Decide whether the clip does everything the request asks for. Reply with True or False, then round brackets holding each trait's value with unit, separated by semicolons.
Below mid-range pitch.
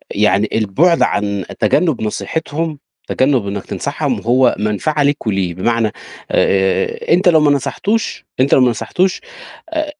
True (130 Hz)